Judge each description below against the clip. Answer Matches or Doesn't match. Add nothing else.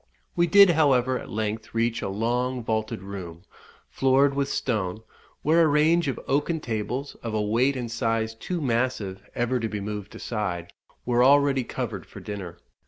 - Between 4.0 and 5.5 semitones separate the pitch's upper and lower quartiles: Matches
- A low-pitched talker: Matches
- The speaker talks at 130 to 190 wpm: Matches